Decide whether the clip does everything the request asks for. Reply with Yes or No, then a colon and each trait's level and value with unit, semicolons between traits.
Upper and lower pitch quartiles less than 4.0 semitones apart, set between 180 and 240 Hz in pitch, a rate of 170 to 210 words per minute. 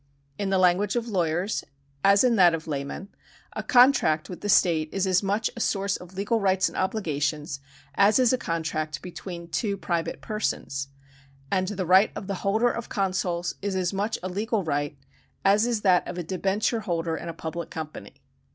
Yes: average, 3.6 semitones; high, 190 Hz; average, 190 wpm